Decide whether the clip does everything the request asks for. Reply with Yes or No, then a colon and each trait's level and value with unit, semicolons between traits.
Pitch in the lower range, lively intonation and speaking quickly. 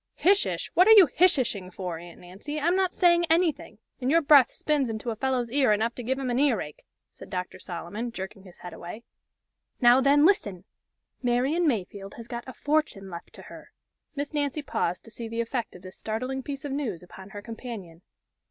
No: high, 240 Hz; wide, 6.6 semitones; fast, 210 wpm